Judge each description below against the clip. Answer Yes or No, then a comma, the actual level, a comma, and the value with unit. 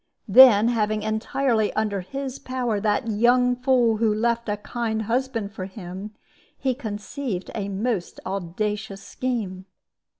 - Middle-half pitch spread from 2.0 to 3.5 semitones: Yes, average, 3.2 semitones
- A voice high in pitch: Yes, high, 220 Hz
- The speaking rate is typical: No, slow, 130 wpm